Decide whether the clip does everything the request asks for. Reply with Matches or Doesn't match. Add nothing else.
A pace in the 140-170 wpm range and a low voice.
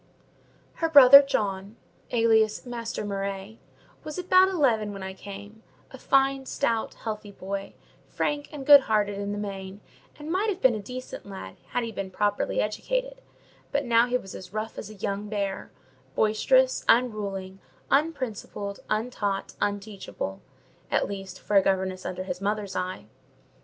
Doesn't match